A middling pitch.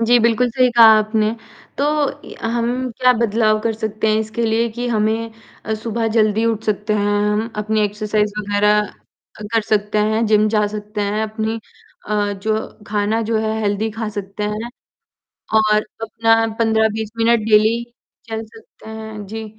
No: high, 220 Hz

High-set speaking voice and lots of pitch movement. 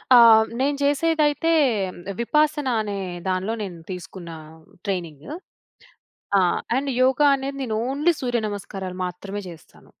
Yes: high, 230 Hz; wide, 6.9 semitones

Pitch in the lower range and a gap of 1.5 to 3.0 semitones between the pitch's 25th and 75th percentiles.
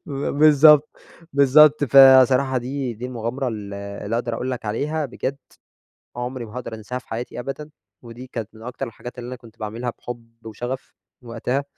Yes: low, 125 Hz; narrow, 2.6 semitones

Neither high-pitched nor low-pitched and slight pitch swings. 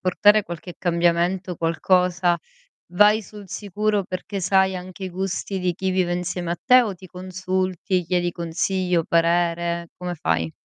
Yes: medium, 180 Hz; narrow, 1.8 semitones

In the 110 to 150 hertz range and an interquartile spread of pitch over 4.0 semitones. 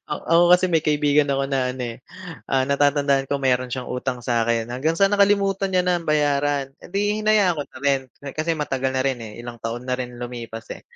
Yes: medium, 140 Hz; average, 4.7 semitones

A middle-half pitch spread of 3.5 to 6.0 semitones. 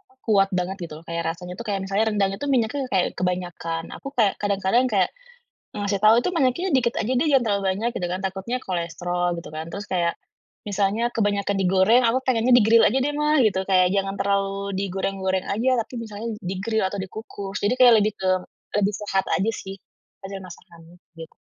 No: average, 2.9 semitones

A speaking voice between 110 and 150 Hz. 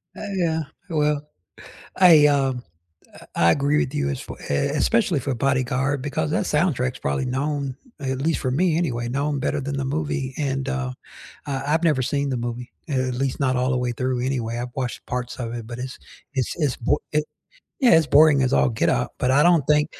Yes: low, 135 Hz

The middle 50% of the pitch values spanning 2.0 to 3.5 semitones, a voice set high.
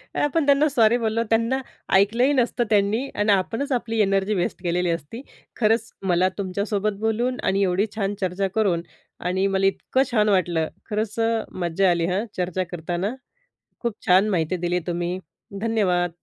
No: average, 3.9 semitones; high, 200 Hz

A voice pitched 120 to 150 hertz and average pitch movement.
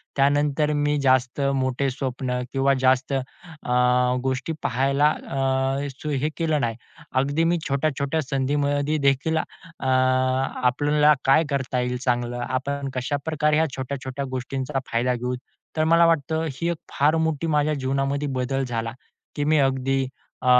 No: low, 135 Hz; narrow, 2.3 semitones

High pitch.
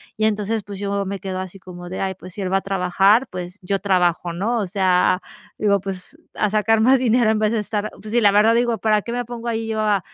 Yes: high, 205 Hz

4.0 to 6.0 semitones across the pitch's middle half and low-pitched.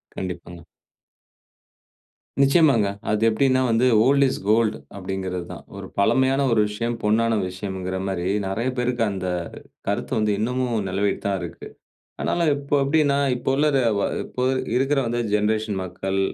Yes: average, 5.1 semitones; low, 110 Hz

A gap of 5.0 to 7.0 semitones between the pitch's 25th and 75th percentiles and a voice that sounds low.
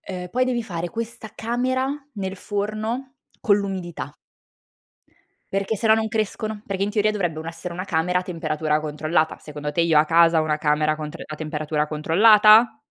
No: wide, 5.5 semitones; medium, 180 Hz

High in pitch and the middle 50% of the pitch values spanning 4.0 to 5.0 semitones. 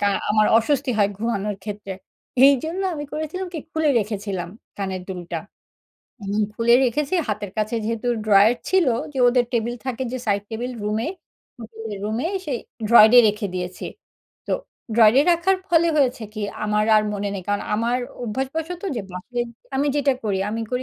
Yes: high, 230 Hz; average, 4.3 semitones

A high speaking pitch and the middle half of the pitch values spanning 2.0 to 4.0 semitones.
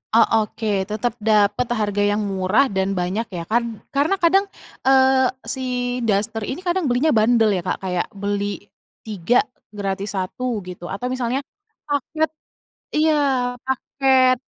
No: high, 230 Hz; average, 4.7 semitones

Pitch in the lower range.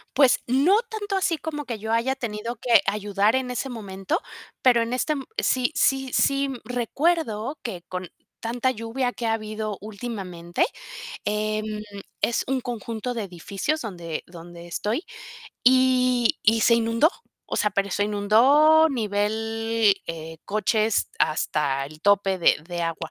No: high, 225 Hz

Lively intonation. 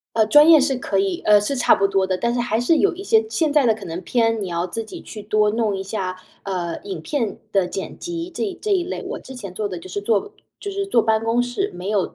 Yes: wide, 7.2 semitones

